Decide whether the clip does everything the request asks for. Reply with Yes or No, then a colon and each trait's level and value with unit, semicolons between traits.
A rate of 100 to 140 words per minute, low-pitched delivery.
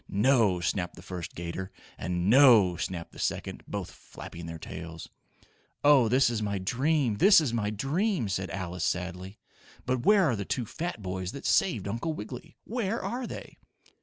No: average, 170 wpm; low, 105 Hz